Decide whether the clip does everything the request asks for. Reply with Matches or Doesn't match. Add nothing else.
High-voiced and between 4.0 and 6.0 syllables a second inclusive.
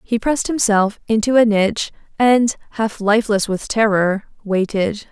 Matches